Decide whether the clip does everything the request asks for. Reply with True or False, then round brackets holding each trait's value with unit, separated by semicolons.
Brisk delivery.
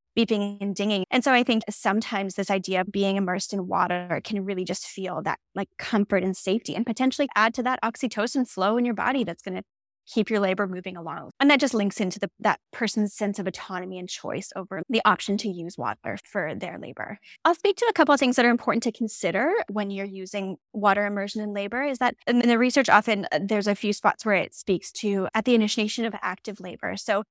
True (230 wpm)